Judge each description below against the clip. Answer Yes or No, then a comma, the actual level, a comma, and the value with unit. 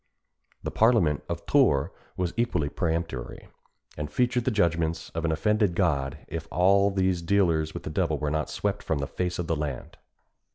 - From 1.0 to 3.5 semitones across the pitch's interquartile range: No, average, 4.1 semitones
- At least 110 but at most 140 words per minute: No, average, 175 wpm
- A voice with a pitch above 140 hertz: No, very low, 85 Hz